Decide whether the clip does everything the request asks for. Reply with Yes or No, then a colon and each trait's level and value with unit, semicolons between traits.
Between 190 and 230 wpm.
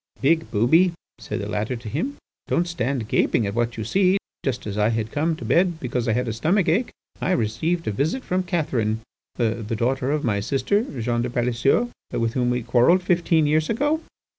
Yes: average, 195 wpm